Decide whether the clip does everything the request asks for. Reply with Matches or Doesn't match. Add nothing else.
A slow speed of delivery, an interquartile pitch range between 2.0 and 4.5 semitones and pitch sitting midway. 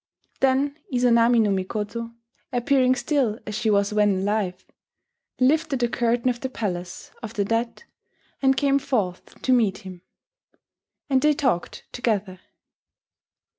Doesn't match